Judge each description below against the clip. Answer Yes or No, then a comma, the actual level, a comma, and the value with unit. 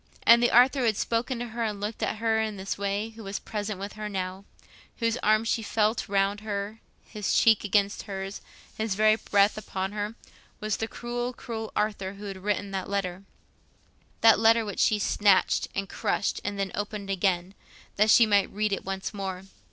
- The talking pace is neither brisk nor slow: Yes, average, 190 wpm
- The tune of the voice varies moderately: No, narrow, 2.0 semitones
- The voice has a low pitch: No, high, 210 Hz